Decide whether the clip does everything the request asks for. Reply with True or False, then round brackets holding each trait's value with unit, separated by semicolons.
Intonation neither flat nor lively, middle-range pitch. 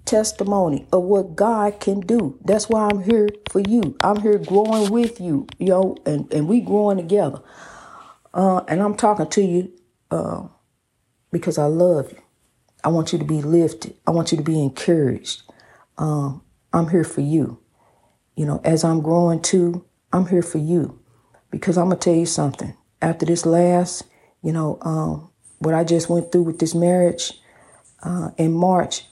True (3.7 semitones; 175 Hz)